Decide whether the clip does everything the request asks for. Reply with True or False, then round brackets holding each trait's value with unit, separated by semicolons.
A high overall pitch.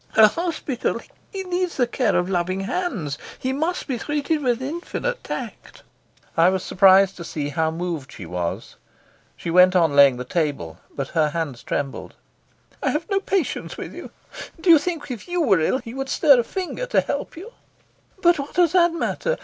True (240 Hz)